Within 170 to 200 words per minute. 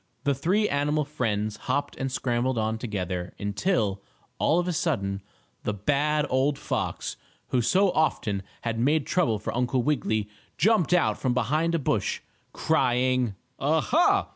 No: average, 150 wpm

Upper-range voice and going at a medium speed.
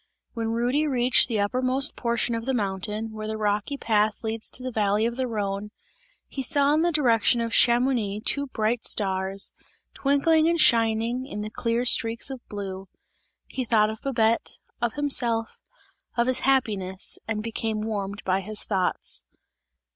Yes: high, 230 Hz; average, 160 wpm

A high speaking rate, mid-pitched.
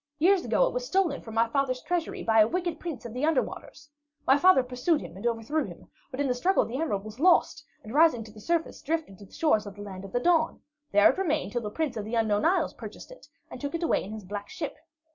No: fast, 265 wpm; very high, 265 Hz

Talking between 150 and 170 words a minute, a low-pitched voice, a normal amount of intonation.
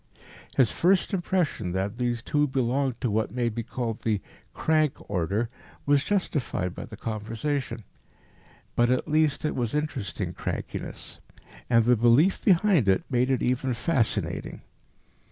No: average, 140 wpm; low, 125 Hz; average, 4.6 semitones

